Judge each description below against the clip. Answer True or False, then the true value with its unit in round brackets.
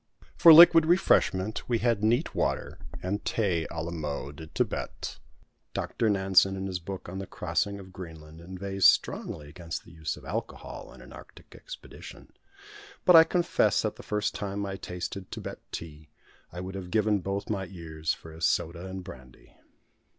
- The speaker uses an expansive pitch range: False (3.6 semitones)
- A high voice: False (95 Hz)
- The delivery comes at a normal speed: True (170 wpm)